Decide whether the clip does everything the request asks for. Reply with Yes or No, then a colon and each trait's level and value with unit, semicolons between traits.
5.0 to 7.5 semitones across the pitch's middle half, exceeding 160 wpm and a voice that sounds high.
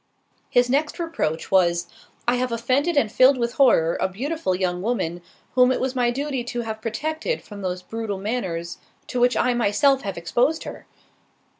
Yes: average, 5.3 semitones; average, 170 wpm; high, 240 Hz